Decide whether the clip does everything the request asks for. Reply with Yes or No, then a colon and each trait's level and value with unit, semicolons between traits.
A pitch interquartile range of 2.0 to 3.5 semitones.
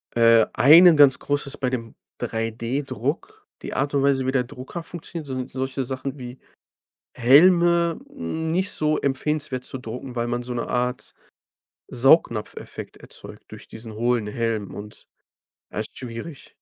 No: average, 4.1 semitones